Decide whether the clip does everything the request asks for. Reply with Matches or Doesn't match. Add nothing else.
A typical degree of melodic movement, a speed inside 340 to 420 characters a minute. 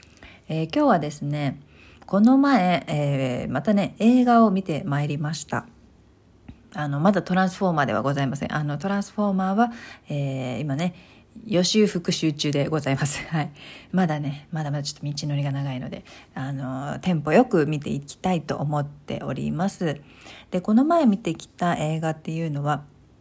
Matches